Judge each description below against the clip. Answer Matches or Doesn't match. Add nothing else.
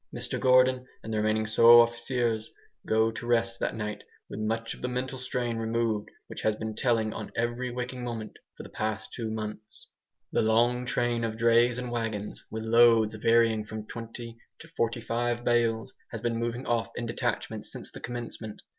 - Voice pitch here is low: Matches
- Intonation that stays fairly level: Matches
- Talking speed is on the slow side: Doesn't match